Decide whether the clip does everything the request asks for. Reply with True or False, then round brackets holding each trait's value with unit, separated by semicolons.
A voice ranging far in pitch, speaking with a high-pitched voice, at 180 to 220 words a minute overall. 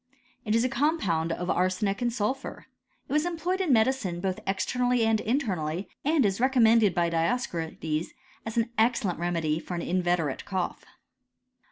False (6.1 semitones; 210 Hz; 165 wpm)